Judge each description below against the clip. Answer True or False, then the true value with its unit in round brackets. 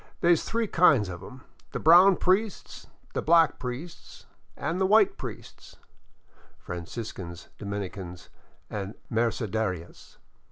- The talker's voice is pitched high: False (120 Hz)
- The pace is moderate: False (120 wpm)